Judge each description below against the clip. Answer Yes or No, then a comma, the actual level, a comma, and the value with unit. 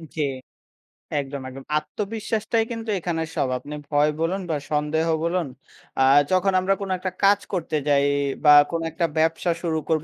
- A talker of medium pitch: Yes, medium, 165 Hz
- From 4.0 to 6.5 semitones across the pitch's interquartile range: Yes, average, 4.3 semitones